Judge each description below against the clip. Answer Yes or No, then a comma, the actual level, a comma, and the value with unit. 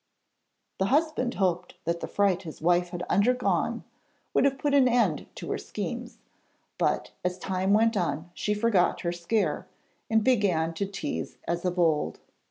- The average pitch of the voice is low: No, high, 190 Hz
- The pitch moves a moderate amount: Yes, average, 4.7 semitones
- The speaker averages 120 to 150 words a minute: No, average, 165 wpm